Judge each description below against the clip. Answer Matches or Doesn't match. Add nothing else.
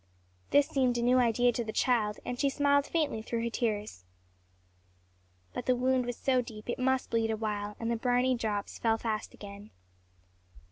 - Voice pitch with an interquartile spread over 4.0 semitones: Doesn't match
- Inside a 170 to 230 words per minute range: Matches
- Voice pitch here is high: Matches